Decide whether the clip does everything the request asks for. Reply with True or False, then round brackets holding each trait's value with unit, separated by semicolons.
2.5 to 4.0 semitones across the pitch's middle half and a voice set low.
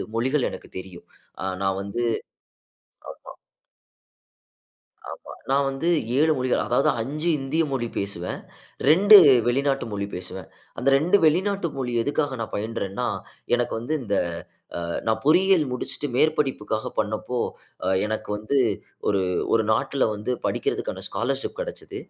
False (5.5 semitones; 130 Hz)